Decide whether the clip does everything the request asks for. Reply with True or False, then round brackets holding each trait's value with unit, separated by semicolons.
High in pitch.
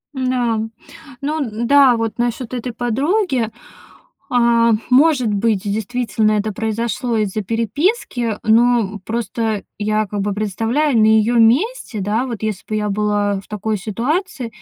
True (230 Hz)